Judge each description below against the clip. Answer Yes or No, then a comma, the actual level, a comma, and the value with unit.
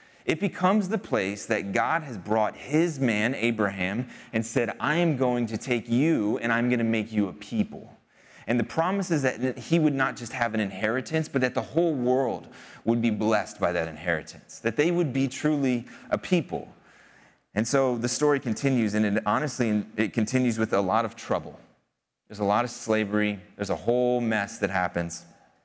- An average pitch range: Yes, average, 3.9 semitones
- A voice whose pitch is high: No, low, 120 Hz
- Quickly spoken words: No, average, 190 wpm